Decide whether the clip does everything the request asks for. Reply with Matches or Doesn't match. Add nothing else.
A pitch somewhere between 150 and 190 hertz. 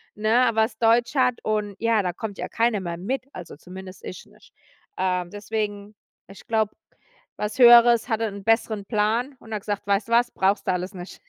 Doesn't match